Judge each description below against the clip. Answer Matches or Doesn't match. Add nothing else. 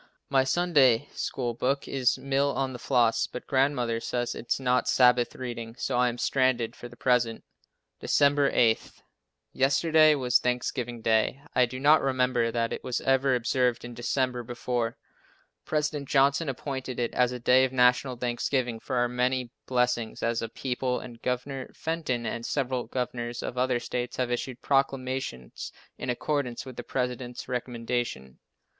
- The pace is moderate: Matches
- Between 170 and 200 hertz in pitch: Doesn't match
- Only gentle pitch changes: Matches